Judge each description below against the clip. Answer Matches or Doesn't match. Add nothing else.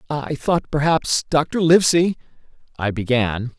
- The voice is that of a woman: Doesn't match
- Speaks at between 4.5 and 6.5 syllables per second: Doesn't match